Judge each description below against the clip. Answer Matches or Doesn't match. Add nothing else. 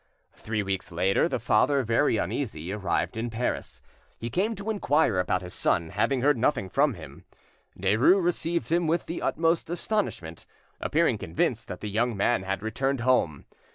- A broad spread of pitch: Matches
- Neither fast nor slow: Matches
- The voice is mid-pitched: Doesn't match